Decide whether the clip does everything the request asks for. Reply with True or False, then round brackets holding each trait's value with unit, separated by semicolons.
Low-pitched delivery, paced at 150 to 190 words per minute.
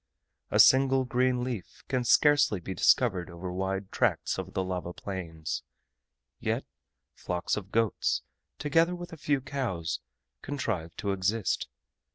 False (105 Hz; 135 wpm)